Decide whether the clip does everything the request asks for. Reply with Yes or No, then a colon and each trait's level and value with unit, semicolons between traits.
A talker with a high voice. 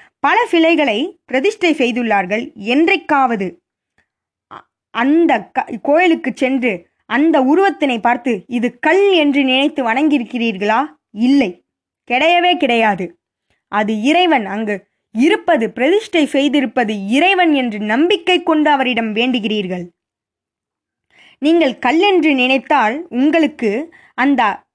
Yes: very high, 275 Hz